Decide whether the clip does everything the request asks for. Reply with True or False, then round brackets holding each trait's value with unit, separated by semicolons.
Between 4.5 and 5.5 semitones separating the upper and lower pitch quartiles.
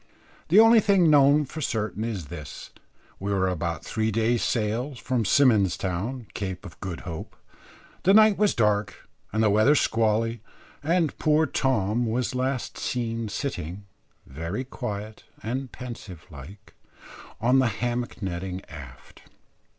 True (5.1 semitones)